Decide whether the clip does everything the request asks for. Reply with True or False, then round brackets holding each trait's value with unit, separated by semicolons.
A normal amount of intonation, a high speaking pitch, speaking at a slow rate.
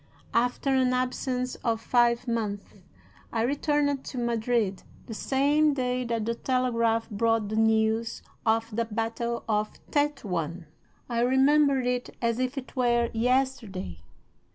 False (2.3 semitones; 235 Hz; 130 wpm)